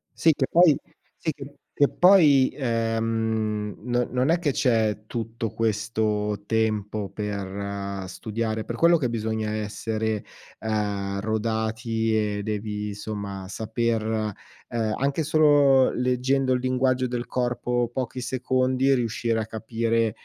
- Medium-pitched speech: No, low, 115 Hz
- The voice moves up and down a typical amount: Yes, average, 3.1 semitones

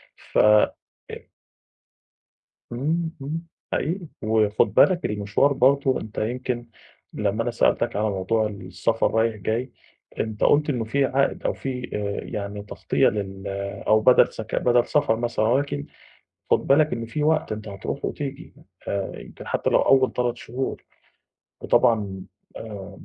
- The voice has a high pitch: No, low, 115 Hz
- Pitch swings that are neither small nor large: Yes, average, 4.2 semitones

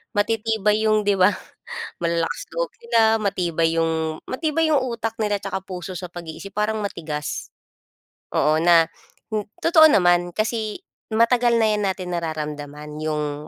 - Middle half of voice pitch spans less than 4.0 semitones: No, average, 5.1 semitones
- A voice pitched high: Yes, high, 195 Hz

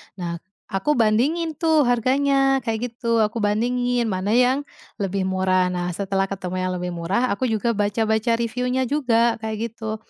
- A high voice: Yes, high, 225 Hz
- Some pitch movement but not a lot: Yes, average, 4.0 semitones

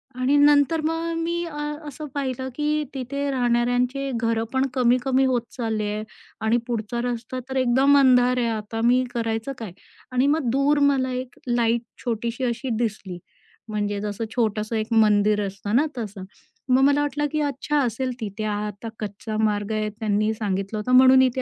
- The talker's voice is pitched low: No, high, 240 Hz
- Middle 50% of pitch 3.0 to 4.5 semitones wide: Yes, average, 3.5 semitones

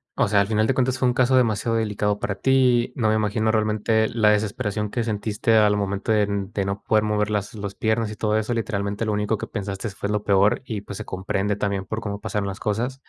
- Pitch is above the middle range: No, low, 105 Hz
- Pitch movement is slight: Yes, narrow, 1.7 semitones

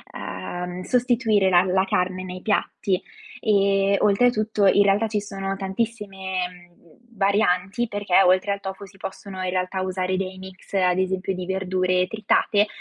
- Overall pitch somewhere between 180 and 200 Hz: Yes, high, 190 Hz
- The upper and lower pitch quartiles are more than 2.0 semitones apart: No, narrow, 1.7 semitones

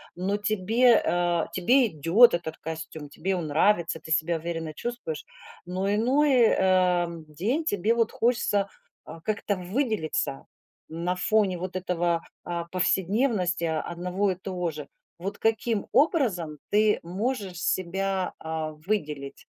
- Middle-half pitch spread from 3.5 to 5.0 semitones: Yes, average, 4.0 semitones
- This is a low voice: No, medium, 185 Hz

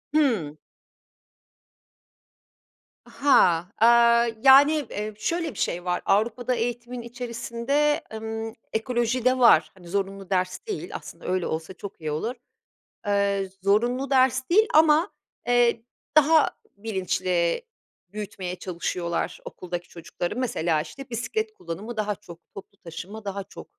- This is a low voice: No, high, 220 Hz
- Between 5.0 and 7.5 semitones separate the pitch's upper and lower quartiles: Yes, average, 5.3 semitones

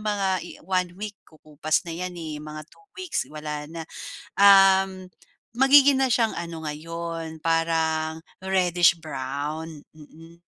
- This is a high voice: No, medium, 165 Hz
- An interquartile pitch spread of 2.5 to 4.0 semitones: Yes, average, 3.4 semitones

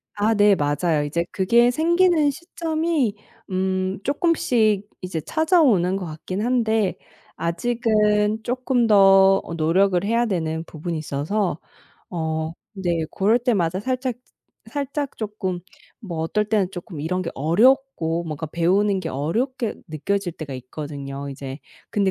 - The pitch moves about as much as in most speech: No, wide, 6.1 semitones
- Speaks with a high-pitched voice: Yes, high, 195 Hz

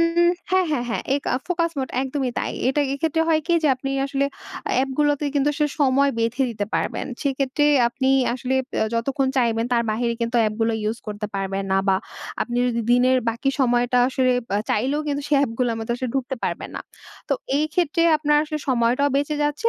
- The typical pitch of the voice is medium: No, very high, 265 Hz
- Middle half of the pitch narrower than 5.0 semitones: Yes, average, 3.8 semitones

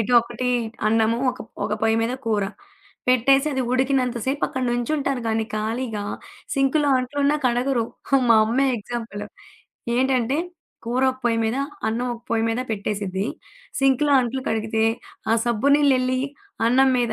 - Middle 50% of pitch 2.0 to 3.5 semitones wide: Yes, average, 2.9 semitones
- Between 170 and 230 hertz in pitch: No, high, 245 Hz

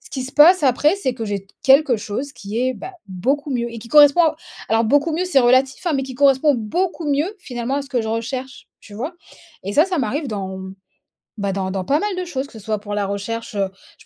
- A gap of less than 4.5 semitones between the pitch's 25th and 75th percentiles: No, average, 5.1 semitones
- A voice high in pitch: Yes, very high, 260 Hz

